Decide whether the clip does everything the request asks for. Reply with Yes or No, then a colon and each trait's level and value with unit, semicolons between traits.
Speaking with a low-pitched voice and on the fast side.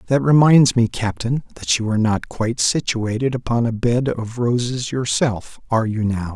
No: low, 120 Hz; average, 180 wpm